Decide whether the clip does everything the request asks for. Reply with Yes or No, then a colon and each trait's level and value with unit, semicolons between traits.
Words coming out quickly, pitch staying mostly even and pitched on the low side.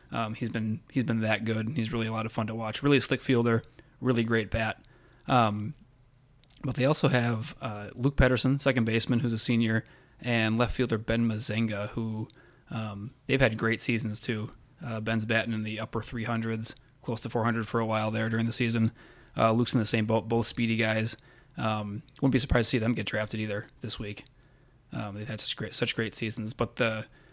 Yes: fast, 210 wpm; narrow, 2.2 semitones; low, 115 Hz